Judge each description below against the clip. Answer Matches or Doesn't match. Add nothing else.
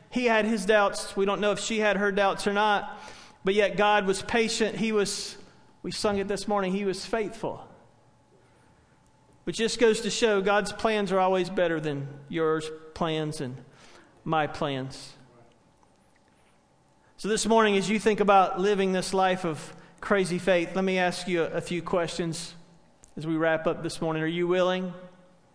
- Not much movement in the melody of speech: Doesn't match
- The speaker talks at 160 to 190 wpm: Matches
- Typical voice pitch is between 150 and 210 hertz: Matches